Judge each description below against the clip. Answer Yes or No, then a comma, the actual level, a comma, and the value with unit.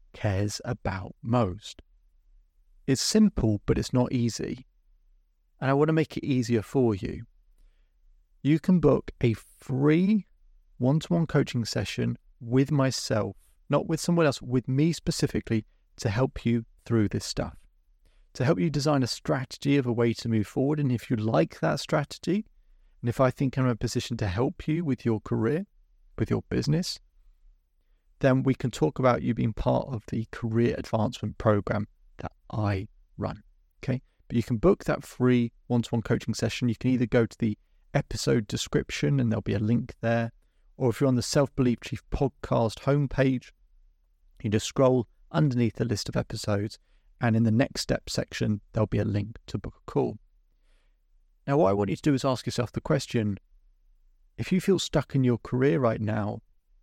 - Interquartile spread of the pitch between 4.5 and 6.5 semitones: Yes, average, 4.9 semitones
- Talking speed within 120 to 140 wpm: No, average, 185 wpm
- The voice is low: Yes, low, 115 Hz